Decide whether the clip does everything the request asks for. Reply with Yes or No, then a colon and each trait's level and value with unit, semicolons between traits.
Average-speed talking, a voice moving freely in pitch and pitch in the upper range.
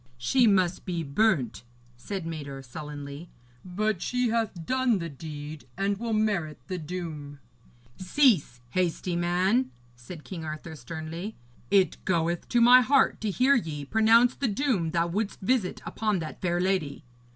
No: average, 150 wpm; wide, 5.8 semitones; medium, 180 Hz